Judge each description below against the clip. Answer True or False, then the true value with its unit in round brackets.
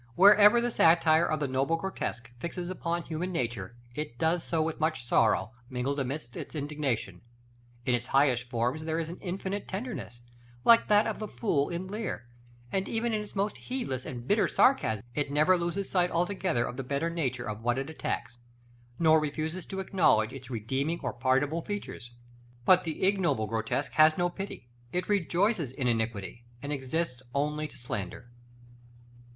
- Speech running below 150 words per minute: False (170 wpm)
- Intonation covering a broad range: True (6.6 semitones)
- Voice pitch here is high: False (155 Hz)